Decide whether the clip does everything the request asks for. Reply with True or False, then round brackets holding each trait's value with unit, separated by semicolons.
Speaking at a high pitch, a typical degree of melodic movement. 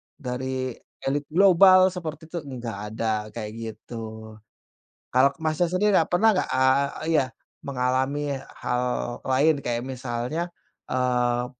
False (130 Hz; 4.6 semitones)